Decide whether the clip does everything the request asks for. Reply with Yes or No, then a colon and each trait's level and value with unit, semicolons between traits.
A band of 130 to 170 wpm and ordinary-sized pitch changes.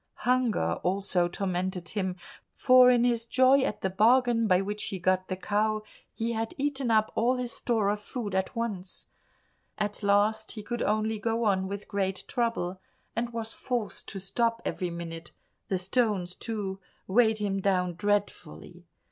Yes: average, 165 wpm; average, 3.6 semitones